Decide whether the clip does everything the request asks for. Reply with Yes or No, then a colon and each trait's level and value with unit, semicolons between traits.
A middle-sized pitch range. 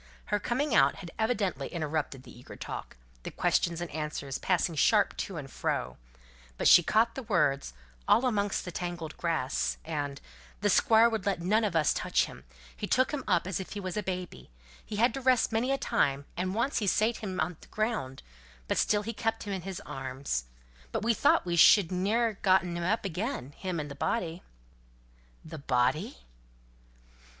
No: wide, 6.0 semitones